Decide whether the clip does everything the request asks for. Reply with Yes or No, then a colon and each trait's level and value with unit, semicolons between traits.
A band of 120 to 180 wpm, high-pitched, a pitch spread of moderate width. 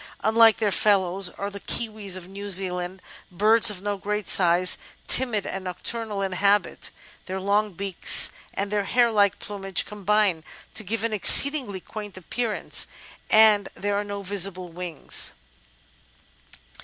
No: average, 145 wpm; high, 200 Hz; narrow, 2.1 semitones